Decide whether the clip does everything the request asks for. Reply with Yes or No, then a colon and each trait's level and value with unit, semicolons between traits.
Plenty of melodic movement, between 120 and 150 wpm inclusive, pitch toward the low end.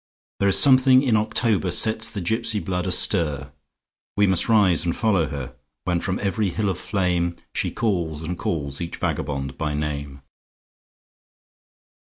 Yes: wide, 6.0 semitones; slow, 135 wpm; very low, 90 Hz